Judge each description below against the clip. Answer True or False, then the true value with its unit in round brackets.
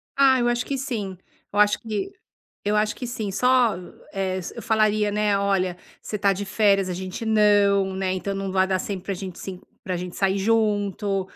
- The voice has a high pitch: True (200 Hz)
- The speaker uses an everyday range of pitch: False (2.0 semitones)